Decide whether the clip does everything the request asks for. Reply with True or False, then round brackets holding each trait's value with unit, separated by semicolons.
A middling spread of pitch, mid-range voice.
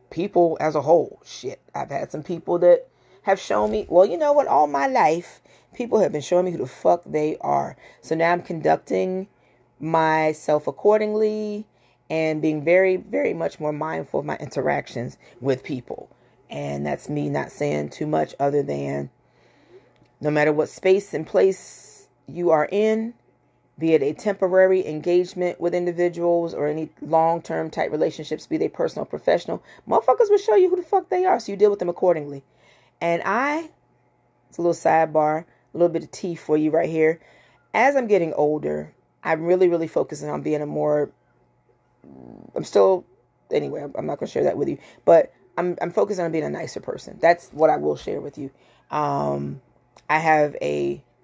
True (4.5 semitones; 160 Hz)